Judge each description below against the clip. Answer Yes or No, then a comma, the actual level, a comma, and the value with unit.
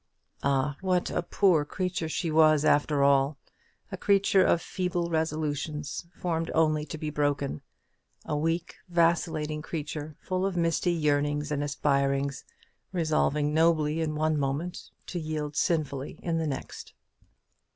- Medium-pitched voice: Yes, medium, 155 Hz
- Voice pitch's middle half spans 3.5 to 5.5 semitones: No, narrow, 2.4 semitones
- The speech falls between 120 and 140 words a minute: Yes, slow, 135 wpm